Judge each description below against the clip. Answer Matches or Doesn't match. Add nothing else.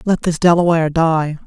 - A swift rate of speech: Doesn't match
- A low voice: Doesn't match